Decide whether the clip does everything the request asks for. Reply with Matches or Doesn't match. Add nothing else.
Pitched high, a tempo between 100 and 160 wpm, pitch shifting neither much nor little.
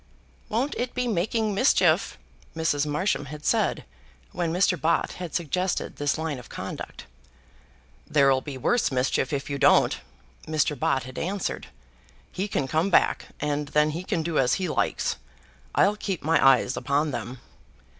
Doesn't match